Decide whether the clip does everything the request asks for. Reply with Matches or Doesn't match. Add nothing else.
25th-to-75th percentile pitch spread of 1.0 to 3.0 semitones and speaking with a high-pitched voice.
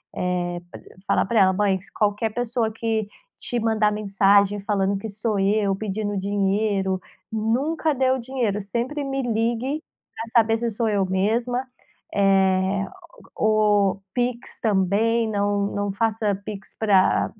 Matches